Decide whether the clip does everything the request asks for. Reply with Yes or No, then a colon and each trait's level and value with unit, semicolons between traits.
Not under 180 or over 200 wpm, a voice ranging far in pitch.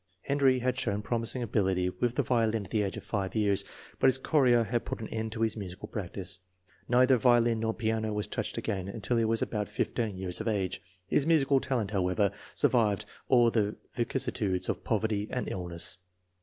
No: average, 190 wpm; average, 3.2 semitones